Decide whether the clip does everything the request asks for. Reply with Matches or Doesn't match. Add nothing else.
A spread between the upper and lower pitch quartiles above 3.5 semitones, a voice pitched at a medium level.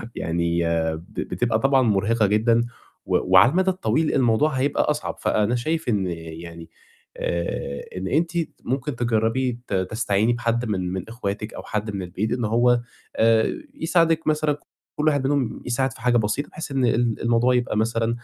Doesn't match